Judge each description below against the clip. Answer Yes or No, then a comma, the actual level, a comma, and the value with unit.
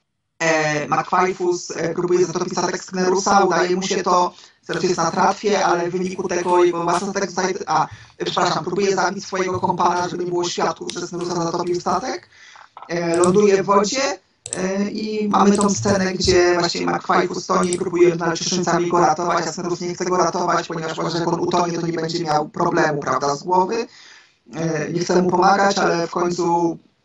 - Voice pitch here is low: No, medium, 180 Hz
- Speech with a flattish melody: Yes, narrow, 1.5 semitones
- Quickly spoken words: Yes, fast, 175 wpm